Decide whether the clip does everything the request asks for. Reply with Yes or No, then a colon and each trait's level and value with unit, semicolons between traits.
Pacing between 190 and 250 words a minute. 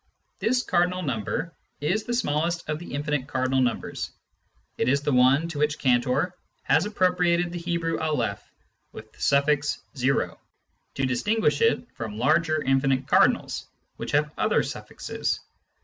No: average, 145 wpm